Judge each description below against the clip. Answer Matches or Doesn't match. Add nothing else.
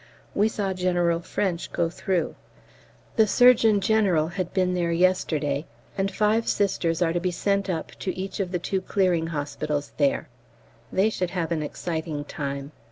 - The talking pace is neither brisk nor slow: Matches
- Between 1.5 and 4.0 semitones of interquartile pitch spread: Matches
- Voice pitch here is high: Doesn't match